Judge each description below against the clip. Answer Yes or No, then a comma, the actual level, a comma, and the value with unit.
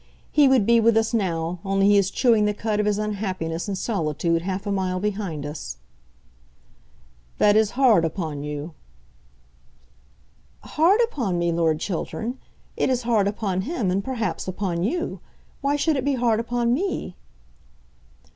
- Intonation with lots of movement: No, average, 4.8 semitones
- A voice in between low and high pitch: No, high, 205 Hz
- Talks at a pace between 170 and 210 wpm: No, average, 155 wpm